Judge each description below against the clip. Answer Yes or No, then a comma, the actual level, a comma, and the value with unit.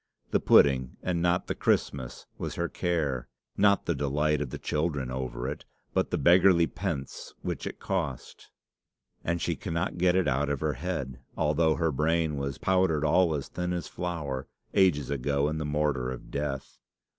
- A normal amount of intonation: Yes, average, 3.8 semitones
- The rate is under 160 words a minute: No, average, 175 wpm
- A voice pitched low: Yes, very low, 75 Hz